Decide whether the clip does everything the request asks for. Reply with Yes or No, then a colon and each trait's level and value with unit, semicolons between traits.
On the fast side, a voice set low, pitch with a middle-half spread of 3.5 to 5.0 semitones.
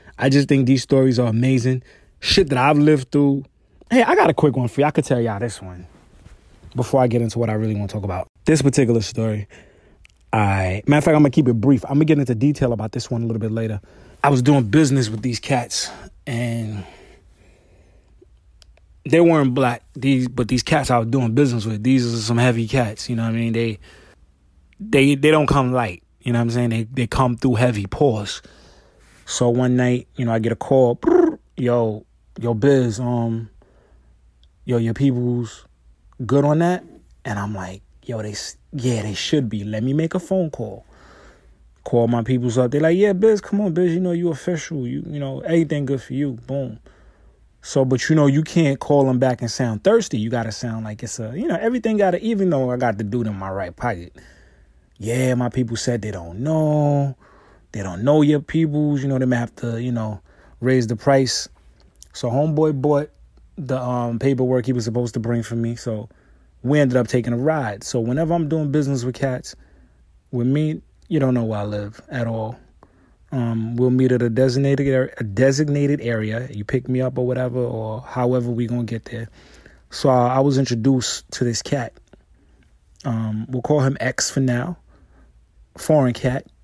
Yes: fast, 210 wpm; low, 125 Hz; average, 4.3 semitones